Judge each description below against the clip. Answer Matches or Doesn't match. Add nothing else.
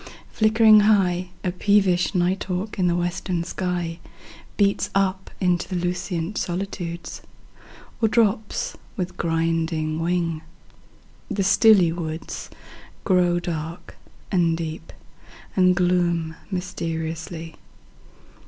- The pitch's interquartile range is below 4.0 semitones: Matches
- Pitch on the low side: Doesn't match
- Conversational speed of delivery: Doesn't match